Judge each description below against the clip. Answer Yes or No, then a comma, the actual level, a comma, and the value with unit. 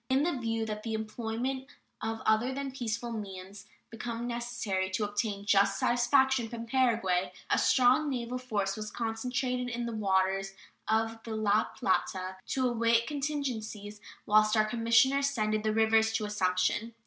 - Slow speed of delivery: No, average, 155 wpm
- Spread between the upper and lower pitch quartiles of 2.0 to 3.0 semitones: Yes, narrow, 2.6 semitones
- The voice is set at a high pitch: Yes, high, 225 Hz